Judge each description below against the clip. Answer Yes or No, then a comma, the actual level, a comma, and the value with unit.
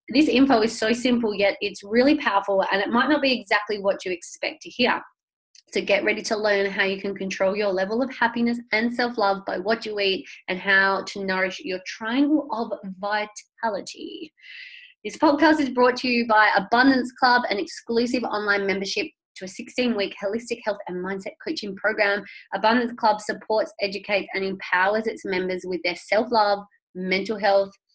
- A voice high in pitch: Yes, high, 215 Hz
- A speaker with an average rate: Yes, average, 185 wpm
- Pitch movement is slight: No, average, 4.0 semitones